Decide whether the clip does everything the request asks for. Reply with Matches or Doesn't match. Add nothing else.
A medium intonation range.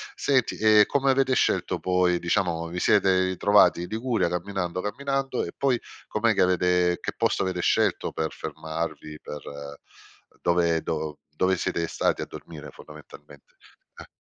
Matches